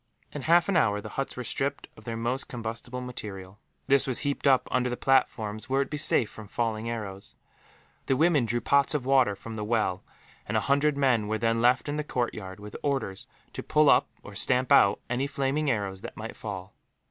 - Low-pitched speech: Yes, low, 120 Hz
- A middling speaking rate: No, fast, 215 wpm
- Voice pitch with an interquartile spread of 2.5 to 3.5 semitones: No, average, 4.2 semitones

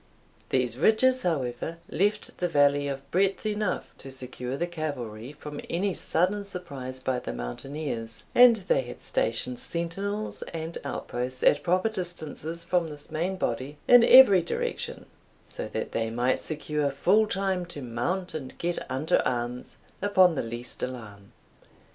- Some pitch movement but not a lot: No, wide, 6.5 semitones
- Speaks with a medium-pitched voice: Yes, medium, 155 Hz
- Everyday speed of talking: Yes, average, 150 wpm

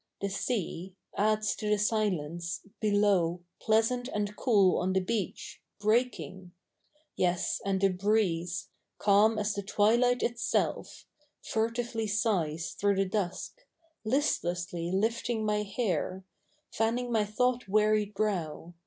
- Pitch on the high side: Yes, high, 205 Hz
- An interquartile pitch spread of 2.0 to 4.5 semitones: Yes, average, 3.1 semitones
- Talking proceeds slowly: Yes, slow, 120 wpm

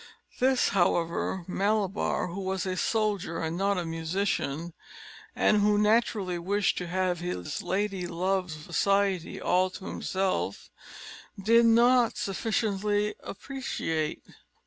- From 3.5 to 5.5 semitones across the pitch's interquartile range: No, average, 3.0 semitones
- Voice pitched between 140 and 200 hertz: Yes, high, 190 Hz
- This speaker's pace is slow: Yes, slow, 115 wpm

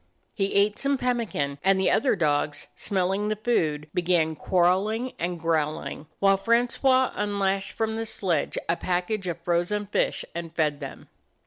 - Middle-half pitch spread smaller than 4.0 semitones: No, average, 4.3 semitones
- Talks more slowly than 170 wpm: Yes, average, 155 wpm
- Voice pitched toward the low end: No, high, 190 Hz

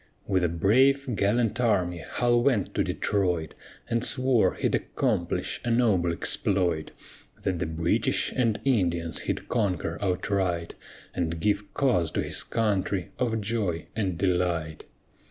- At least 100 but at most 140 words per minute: Yes, slow, 135 wpm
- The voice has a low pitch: Yes, low, 100 Hz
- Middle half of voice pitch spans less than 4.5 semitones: No, average, 5.1 semitones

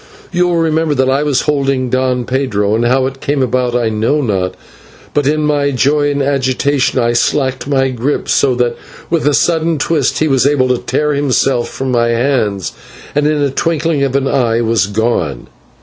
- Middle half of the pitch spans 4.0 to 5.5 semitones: No, average, 3.2 semitones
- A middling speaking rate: Yes, average, 195 wpm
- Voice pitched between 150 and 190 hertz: No, low, 135 Hz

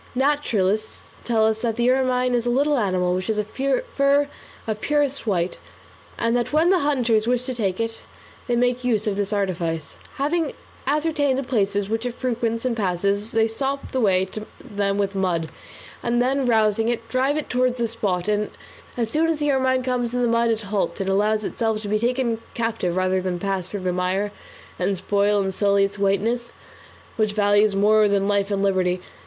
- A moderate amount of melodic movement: Yes, average, 3.9 semitones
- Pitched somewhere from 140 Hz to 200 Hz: No, high, 220 Hz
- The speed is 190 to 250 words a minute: Yes, average, 200 wpm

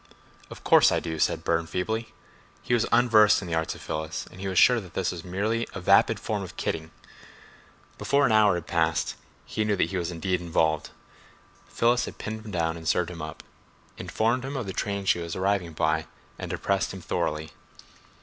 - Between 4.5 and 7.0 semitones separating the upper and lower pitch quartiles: Yes, average, 4.8 semitones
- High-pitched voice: No, very low, 90 Hz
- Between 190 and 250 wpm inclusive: Yes, average, 200 wpm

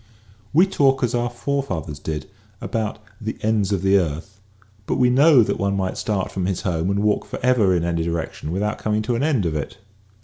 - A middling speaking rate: No, fast, 215 wpm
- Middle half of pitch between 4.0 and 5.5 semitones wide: Yes, average, 5.2 semitones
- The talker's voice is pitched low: Yes, low, 100 Hz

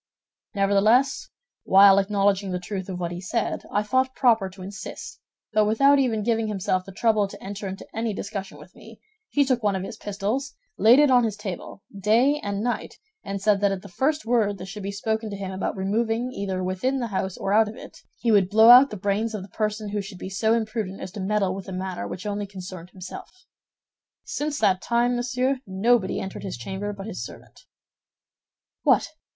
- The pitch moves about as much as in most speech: Yes, average, 3.0 semitones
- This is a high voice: Yes, high, 205 Hz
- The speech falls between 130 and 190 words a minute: No, fast, 205 wpm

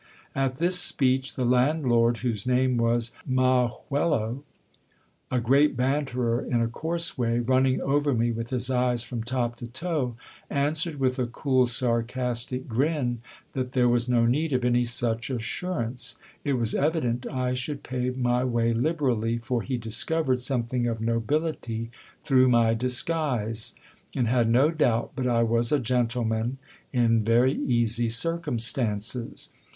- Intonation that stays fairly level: Yes, narrow, 2.2 semitones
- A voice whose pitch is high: No, low, 125 Hz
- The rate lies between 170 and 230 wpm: No, average, 150 wpm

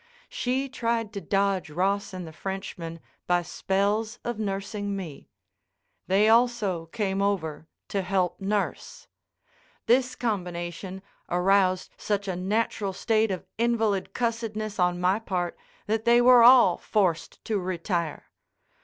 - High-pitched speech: Yes, high, 200 Hz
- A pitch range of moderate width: Yes, average, 3.4 semitones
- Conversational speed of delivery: No, slow, 125 wpm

